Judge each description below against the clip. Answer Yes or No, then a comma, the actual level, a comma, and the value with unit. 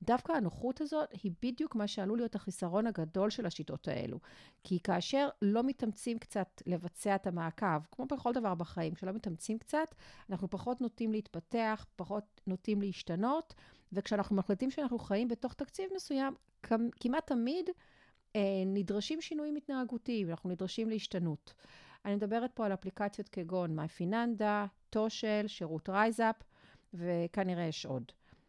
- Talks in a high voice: Yes, high, 210 Hz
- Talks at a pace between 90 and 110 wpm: No, average, 135 wpm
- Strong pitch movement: No, average, 4.5 semitones